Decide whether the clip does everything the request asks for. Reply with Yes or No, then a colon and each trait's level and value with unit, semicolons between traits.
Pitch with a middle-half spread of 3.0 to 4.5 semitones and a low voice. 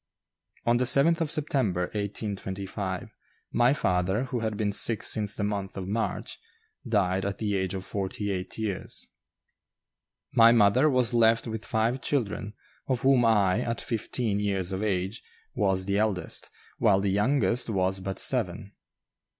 Yes: average, 3.4 semitones; low, 105 Hz